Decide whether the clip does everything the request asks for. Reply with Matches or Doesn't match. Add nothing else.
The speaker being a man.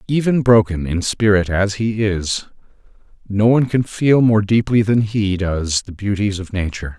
Matches